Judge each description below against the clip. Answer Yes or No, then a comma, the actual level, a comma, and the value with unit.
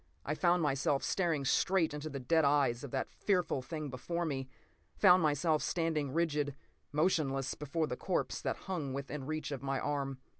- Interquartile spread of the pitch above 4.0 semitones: No, average, 3.1 semitones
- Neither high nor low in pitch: Yes, medium, 150 Hz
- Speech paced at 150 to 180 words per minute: Yes, average, 175 wpm